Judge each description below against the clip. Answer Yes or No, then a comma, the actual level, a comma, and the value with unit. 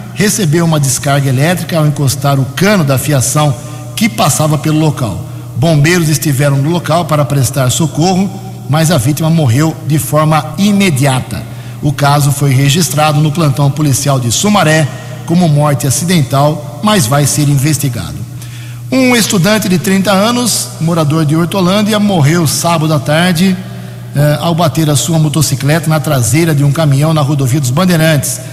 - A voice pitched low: No, medium, 150 Hz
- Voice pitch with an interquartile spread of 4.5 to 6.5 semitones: No, average, 3.2 semitones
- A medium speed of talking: Yes, average, 150 wpm